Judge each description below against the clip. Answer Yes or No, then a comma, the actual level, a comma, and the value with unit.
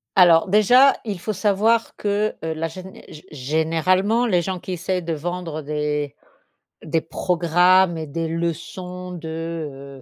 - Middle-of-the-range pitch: Yes, medium, 170 Hz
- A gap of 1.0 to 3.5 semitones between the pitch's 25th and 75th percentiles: Yes, average, 2.9 semitones